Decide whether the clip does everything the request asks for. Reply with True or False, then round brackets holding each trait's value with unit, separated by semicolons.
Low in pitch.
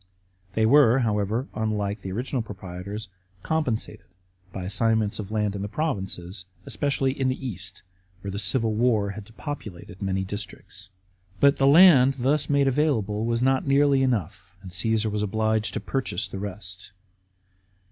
True (110 Hz)